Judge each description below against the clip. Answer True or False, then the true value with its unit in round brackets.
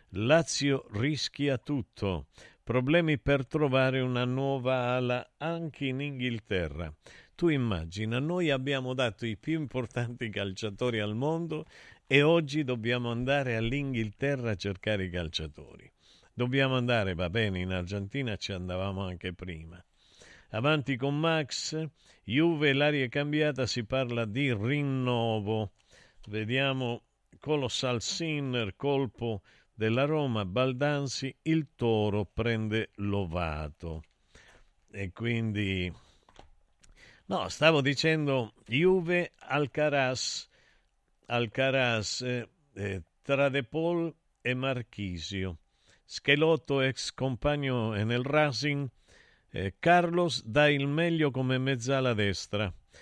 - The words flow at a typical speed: False (100 wpm)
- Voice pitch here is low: True (125 Hz)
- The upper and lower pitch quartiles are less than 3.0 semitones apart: False (5.1 semitones)